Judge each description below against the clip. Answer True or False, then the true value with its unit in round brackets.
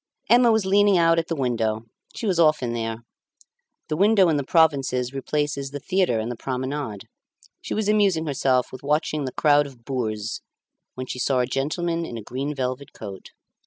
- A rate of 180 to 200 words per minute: True (185 wpm)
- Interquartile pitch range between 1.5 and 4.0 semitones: False (4.8 semitones)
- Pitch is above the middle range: False (140 Hz)